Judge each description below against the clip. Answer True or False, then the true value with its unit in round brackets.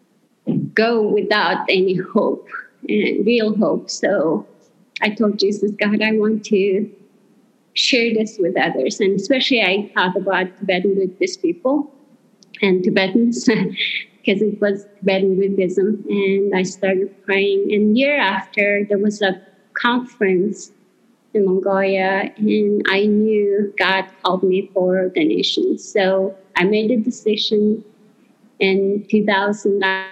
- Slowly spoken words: True (130 wpm)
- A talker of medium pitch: False (205 Hz)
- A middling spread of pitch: False (2.0 semitones)